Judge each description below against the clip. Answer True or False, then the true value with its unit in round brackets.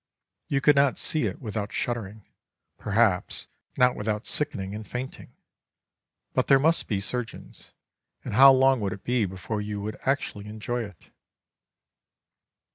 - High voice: False (110 Hz)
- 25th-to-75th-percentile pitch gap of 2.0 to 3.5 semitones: False (4.2 semitones)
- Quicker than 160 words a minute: False (140 wpm)